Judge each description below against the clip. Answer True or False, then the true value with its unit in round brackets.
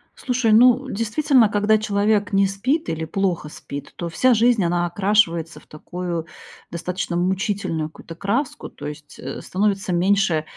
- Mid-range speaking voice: False (195 Hz)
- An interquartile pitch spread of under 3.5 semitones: False (4.1 semitones)